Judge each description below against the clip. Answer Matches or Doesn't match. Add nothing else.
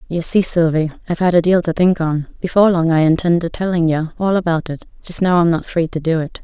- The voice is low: Doesn't match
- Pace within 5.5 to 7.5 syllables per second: Matches